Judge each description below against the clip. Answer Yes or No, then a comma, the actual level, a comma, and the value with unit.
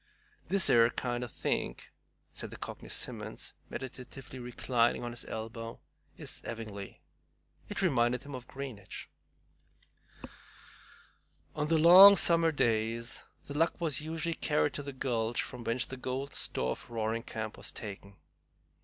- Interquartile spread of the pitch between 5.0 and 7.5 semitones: No, average, 4.2 semitones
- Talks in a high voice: No, low, 125 Hz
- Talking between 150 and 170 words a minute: No, average, 140 wpm